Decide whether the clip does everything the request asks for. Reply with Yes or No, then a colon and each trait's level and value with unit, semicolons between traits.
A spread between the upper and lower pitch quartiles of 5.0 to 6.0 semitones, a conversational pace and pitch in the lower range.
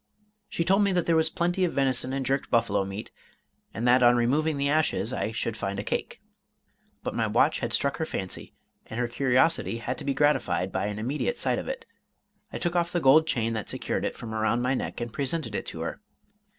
No: wide, 5.6 semitones; fast, 225 wpm; low, 130 Hz